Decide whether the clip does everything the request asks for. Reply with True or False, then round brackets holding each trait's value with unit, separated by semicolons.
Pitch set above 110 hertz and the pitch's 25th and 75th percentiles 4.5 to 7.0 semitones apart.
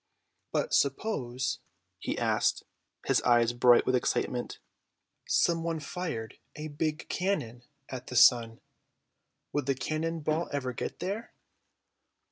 True (140 Hz; 5.1 semitones)